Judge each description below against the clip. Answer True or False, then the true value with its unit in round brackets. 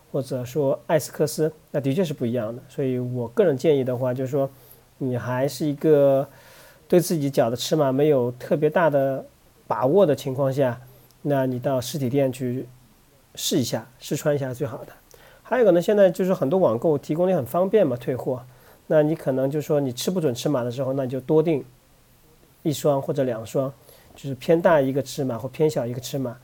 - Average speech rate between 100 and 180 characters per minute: False (300 characters per minute)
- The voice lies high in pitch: False (140 Hz)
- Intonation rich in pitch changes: False (3.2 semitones)